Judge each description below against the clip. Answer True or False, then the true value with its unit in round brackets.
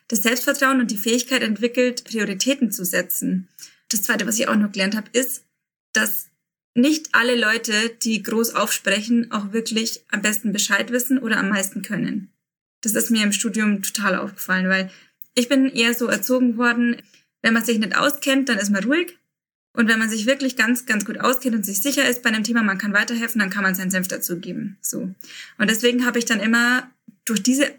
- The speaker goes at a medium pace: False (200 wpm)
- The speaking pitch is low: False (230 Hz)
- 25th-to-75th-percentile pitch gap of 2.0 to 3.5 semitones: True (3.0 semitones)